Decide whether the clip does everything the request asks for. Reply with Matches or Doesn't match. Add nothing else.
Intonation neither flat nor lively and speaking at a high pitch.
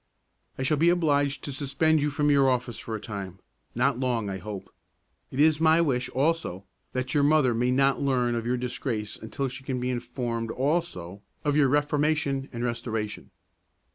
Doesn't match